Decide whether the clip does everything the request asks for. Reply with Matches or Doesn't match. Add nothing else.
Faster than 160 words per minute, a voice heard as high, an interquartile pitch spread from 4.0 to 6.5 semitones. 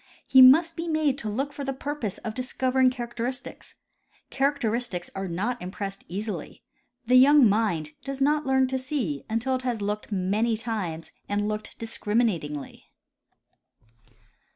Doesn't match